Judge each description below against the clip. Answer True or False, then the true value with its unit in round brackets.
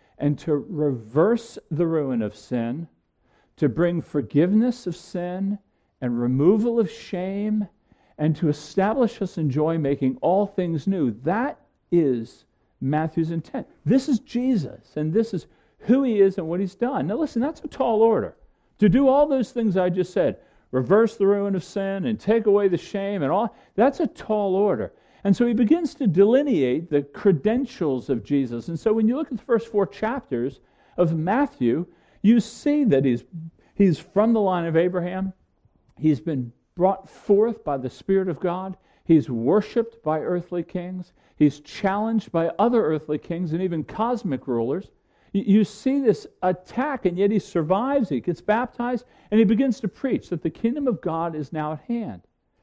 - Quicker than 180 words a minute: False (175 wpm)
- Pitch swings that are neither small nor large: False (6.0 semitones)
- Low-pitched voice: False (190 Hz)